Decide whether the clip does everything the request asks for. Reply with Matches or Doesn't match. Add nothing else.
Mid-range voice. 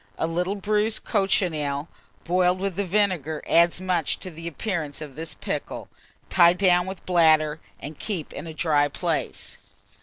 Matches